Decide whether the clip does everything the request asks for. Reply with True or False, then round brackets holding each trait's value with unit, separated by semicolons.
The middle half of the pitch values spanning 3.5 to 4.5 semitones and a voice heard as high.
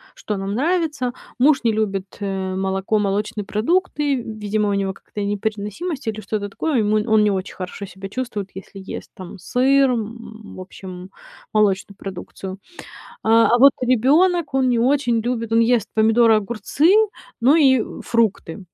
True (4.1 semitones; 220 Hz)